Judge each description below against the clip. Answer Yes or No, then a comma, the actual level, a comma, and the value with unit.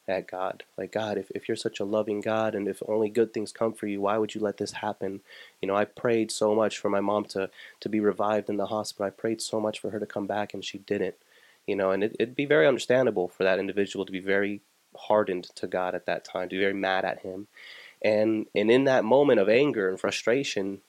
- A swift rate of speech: Yes, fast, 255 wpm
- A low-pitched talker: Yes, low, 105 Hz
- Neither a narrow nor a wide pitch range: No, narrow, 1.6 semitones